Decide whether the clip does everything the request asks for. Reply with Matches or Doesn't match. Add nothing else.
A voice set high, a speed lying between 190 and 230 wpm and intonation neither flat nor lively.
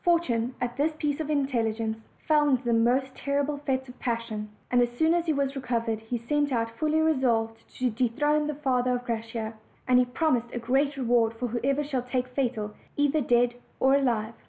Matches